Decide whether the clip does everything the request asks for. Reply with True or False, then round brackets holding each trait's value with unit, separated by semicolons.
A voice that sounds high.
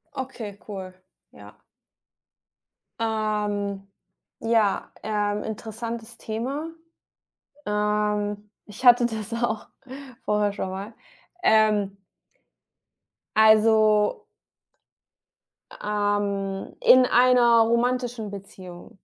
True (215 Hz)